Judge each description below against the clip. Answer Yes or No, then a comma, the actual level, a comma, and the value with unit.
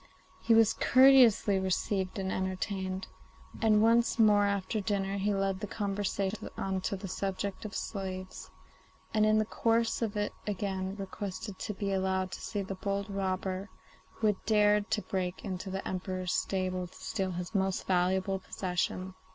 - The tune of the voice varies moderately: No, narrow, 1.8 semitones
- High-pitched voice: Yes, high, 195 Hz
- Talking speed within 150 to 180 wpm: Yes, average, 160 wpm